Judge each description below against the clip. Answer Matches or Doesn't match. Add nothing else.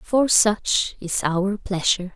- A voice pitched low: Doesn't match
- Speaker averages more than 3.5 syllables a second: Doesn't match